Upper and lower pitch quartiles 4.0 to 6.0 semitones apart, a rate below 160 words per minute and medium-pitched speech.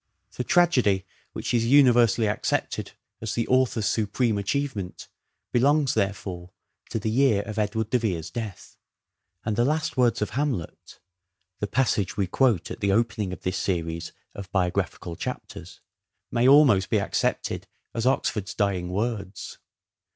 No: average, 4.4 semitones; average, 150 wpm; low, 105 Hz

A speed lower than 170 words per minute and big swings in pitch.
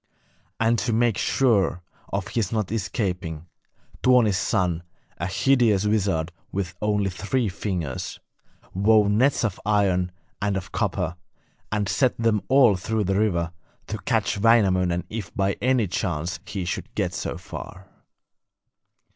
No: slow, 135 wpm; average, 3.4 semitones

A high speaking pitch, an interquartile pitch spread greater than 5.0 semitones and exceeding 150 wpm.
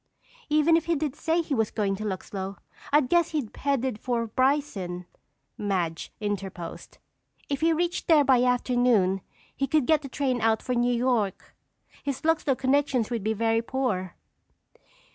Yes: very high, 250 Hz; wide, 5.4 semitones; average, 160 wpm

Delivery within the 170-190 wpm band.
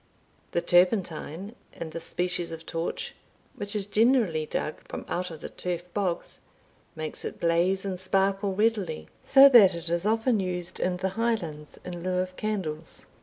No: average, 160 wpm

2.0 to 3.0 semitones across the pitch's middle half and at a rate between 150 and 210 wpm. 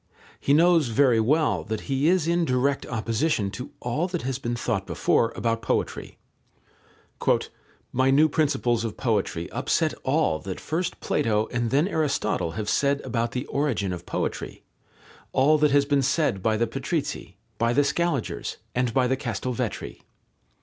No: average, 4.3 semitones; average, 155 wpm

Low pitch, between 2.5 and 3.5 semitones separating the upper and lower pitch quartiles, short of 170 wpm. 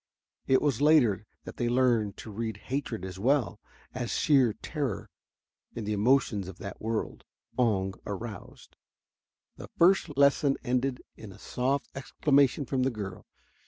No: low, 120 Hz; average, 4.6 semitones; average, 145 wpm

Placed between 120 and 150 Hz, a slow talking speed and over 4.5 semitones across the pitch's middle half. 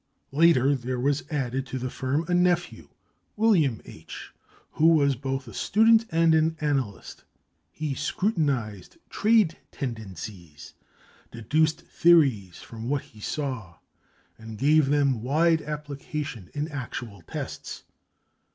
Yes: medium, 140 Hz; slow, 120 wpm; average, 4.9 semitones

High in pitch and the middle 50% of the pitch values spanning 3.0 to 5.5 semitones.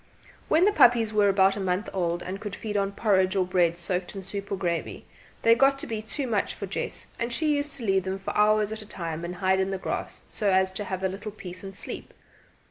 No: high, 195 Hz; narrow, 2.5 semitones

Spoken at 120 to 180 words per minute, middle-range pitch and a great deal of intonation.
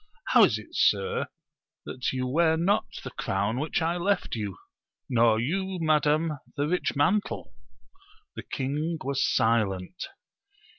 Yes: slow, 135 wpm; medium, 150 Hz; wide, 5.8 semitones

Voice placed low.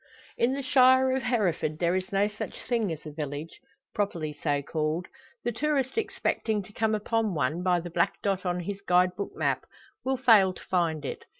No: high, 190 Hz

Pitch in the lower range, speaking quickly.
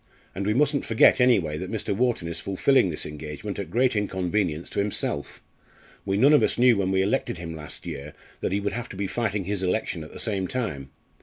Yes: low, 100 Hz; fast, 220 wpm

